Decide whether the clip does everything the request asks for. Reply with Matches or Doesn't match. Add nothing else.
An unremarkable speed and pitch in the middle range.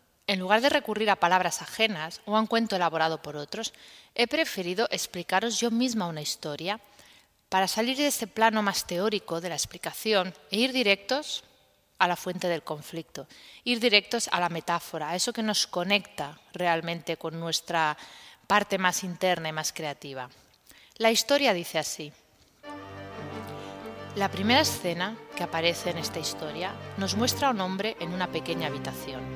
Matches